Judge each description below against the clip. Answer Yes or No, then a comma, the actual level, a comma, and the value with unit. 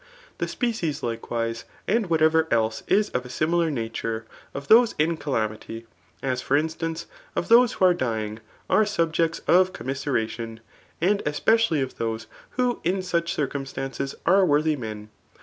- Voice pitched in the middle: Yes, medium, 150 Hz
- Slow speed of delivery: No, average, 150 wpm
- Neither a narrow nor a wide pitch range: No, wide, 7.0 semitones